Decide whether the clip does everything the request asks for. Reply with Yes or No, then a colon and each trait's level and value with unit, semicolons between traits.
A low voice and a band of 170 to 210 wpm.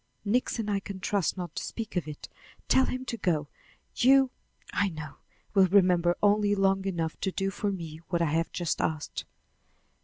No: high, 190 Hz; average, 180 wpm